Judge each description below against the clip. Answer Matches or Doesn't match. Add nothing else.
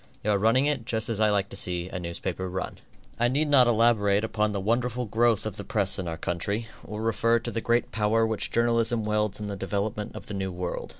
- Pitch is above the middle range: Doesn't match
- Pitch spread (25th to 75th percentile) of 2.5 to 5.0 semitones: Matches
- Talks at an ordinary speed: Doesn't match